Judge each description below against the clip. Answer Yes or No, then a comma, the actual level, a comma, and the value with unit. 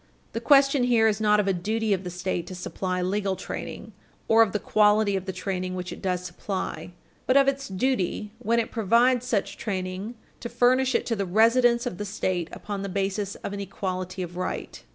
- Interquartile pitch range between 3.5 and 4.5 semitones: Yes, average, 3.8 semitones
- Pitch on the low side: No, high, 200 Hz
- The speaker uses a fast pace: Yes, fast, 210 wpm